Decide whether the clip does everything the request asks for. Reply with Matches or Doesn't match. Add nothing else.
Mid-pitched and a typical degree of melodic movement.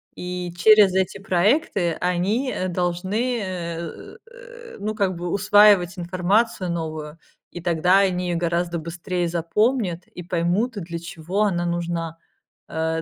Matches